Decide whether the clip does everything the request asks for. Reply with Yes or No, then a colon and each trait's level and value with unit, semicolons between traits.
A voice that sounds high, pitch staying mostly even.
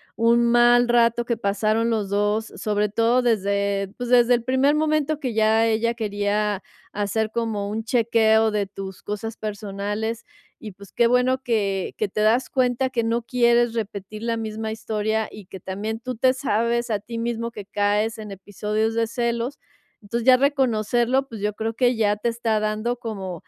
Yes: high, 225 Hz; narrow, 2.2 semitones